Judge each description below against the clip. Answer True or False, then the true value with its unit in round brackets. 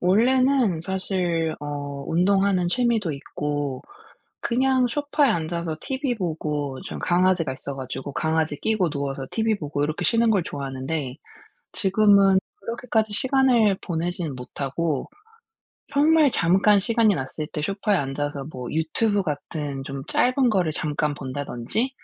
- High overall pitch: False (175 Hz)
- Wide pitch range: True (7.1 semitones)